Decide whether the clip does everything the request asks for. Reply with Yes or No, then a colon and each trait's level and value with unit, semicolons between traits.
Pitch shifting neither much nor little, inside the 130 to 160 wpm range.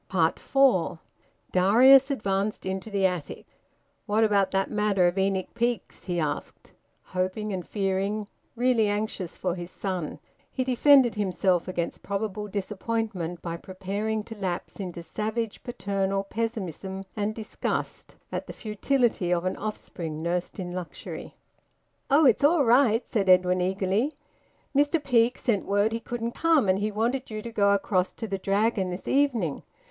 Yes: average, 3.6 semitones; average, 150 wpm